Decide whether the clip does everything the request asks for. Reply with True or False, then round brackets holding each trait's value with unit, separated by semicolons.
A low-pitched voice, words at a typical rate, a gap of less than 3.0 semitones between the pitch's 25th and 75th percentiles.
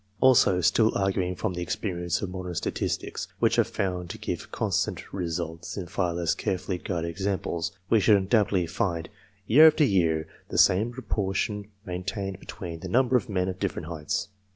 True (95 Hz; 170 wpm; 2.6 semitones)